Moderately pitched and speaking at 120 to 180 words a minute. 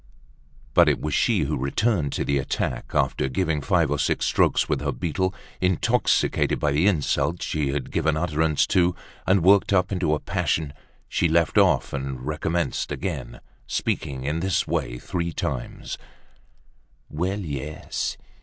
No: very low, 80 Hz; average, 155 wpm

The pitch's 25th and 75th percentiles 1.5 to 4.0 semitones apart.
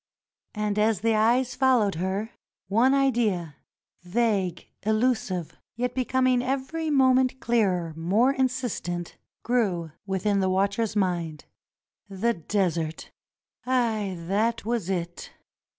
No: average, 5.0 semitones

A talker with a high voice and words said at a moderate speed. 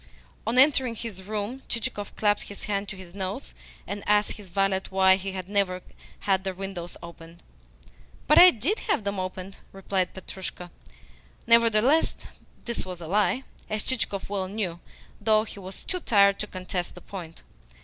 Yes: high, 200 Hz; average, 165 wpm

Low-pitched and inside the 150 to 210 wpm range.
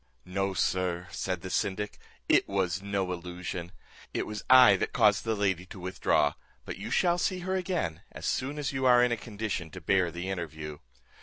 Yes: very low, 95 Hz; average, 190 wpm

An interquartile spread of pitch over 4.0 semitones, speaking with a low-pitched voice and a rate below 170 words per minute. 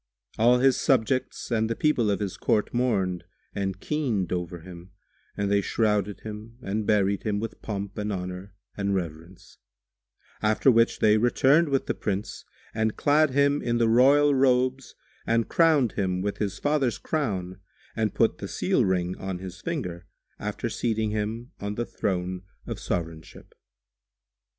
Yes: average, 4.5 semitones; low, 105 Hz; average, 155 wpm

